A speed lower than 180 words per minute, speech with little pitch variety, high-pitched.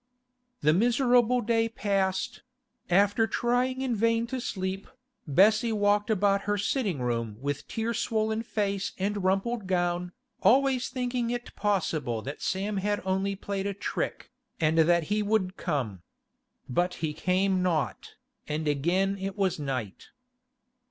No: average, 140 wpm; average, 4.2 semitones; high, 195 Hz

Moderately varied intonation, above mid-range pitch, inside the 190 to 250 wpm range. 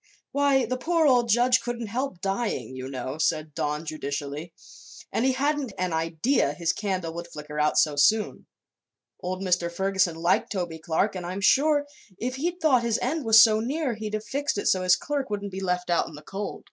No: wide, 7.2 semitones; high, 195 Hz; fast, 205 wpm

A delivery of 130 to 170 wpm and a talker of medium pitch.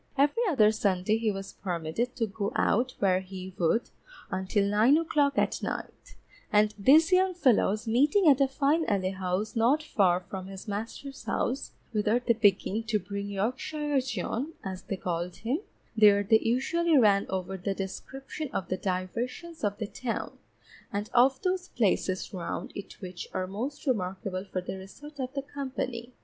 No: average, 160 wpm; high, 215 Hz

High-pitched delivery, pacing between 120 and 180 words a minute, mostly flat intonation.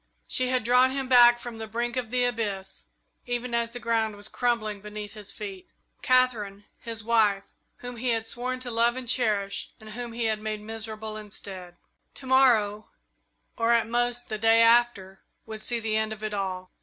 No: high, 225 Hz; average, 195 wpm; narrow, 2.3 semitones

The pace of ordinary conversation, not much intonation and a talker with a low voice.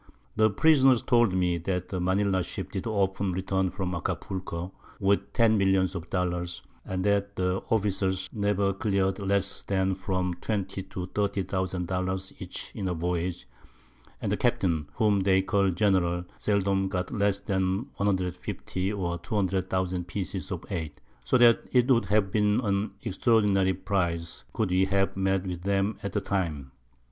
Yes: average, 155 wpm; narrow, 1.7 semitones; very low, 95 Hz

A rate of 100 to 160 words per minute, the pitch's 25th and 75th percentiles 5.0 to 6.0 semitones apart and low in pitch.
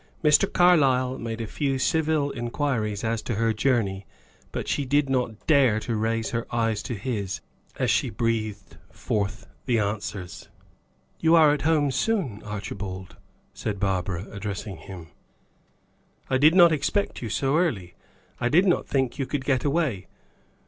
Yes: average, 155 wpm; wide, 5.6 semitones; low, 120 Hz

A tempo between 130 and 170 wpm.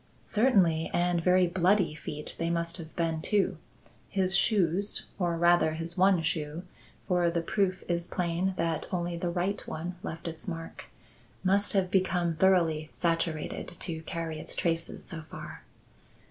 Yes: average, 150 wpm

